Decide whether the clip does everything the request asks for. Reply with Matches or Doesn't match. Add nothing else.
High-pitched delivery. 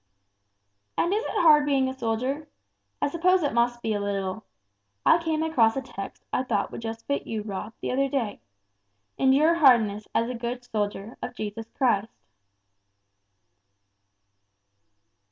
Matches